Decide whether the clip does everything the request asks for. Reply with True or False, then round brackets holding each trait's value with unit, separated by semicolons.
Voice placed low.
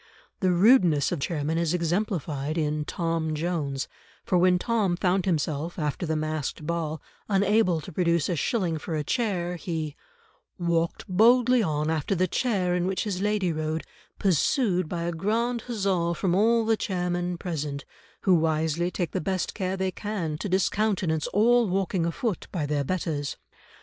False (175 Hz)